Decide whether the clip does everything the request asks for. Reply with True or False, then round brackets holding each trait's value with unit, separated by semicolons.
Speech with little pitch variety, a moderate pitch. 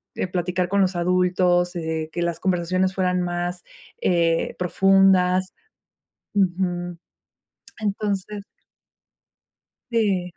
True (1.4 semitones; 180 Hz)